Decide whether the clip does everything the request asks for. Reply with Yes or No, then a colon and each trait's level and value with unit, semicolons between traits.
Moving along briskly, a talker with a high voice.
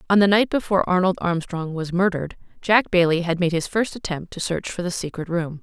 No: fast, 225 wpm; medium, 180 Hz